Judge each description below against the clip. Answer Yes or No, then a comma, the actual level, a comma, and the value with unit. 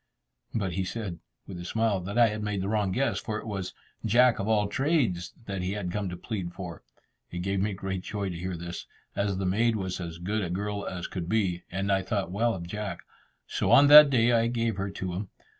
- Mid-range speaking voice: No, low, 100 Hz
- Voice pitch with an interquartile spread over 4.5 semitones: No, average, 3.1 semitones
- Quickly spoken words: Yes, fast, 235 wpm